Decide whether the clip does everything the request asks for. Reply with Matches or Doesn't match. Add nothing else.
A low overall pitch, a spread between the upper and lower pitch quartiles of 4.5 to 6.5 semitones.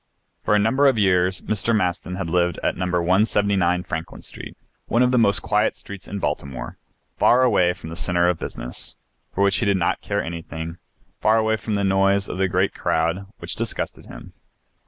Doesn't match